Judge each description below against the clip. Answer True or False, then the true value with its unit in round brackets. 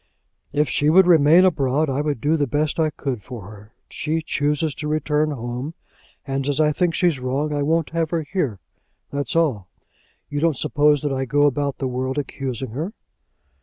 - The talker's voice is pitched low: False (145 Hz)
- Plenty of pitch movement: False (2.8 semitones)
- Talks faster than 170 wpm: True (190 wpm)